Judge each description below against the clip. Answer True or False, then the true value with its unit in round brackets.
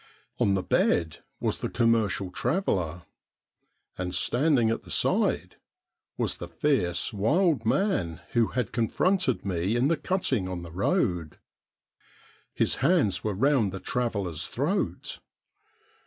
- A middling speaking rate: False (125 wpm)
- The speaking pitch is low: True (105 Hz)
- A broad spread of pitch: True (7.2 semitones)